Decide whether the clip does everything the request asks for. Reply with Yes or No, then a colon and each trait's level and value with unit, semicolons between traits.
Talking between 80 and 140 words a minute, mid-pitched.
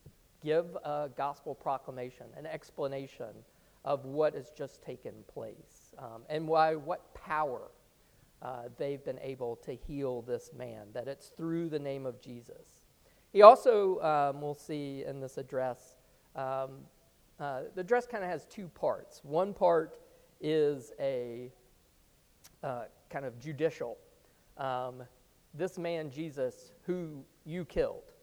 Yes: slow, 135 wpm; medium, 145 Hz